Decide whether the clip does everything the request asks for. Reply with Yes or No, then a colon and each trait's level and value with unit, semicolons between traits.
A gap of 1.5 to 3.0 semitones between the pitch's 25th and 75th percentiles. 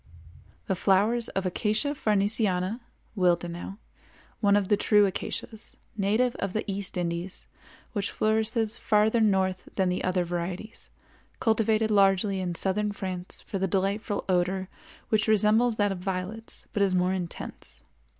Yes: average, 2.7 semitones